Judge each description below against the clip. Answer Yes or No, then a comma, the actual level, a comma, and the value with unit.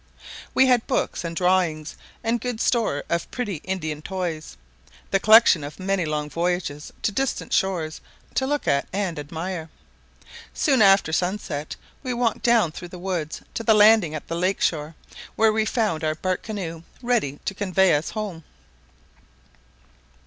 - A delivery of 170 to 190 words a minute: No, average, 160 wpm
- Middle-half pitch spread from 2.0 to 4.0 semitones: No, average, 5.3 semitones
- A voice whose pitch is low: No, medium, 185 Hz